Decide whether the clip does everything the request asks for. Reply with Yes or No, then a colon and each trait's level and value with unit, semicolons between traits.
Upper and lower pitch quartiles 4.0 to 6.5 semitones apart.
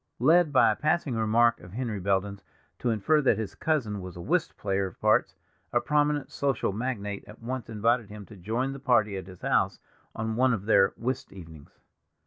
Yes: average, 4.7 semitones